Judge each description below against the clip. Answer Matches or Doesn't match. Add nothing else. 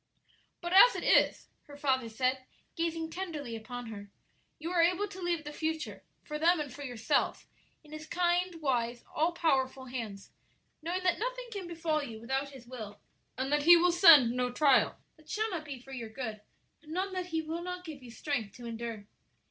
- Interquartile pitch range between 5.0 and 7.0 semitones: Matches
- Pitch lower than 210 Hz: Doesn't match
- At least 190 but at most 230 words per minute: Matches